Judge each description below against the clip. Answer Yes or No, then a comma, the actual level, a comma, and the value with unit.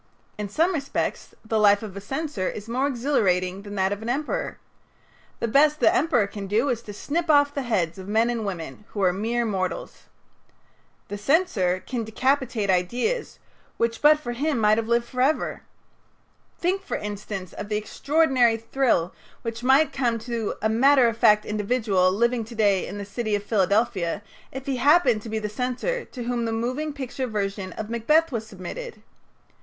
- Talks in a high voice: Yes, high, 230 Hz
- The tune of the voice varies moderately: Yes, average, 4.6 semitones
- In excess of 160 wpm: Yes, average, 180 wpm